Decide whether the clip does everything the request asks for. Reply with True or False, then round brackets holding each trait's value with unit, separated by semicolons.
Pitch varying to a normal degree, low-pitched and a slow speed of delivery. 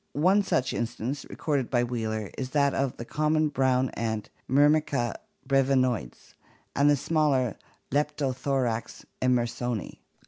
True (3.1 semitones; 130 Hz; 130 wpm)